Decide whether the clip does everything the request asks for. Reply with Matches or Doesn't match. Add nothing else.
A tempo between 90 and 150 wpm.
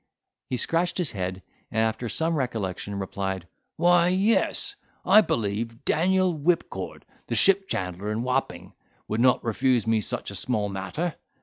Matches